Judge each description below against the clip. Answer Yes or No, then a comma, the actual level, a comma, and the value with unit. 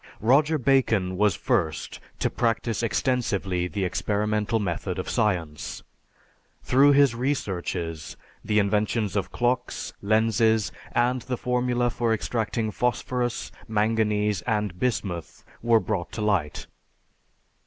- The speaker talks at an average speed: No, slow, 110 wpm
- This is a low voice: Yes, low, 110 Hz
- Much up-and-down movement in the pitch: No, average, 3.6 semitones